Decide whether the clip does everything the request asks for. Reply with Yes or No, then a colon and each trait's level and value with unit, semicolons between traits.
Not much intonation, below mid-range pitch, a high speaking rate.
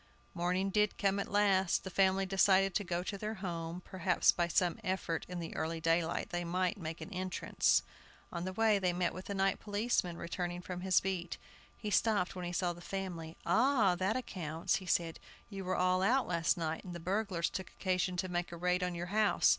No: narrow, 2.0 semitones; medium, 185 Hz; fast, 210 wpm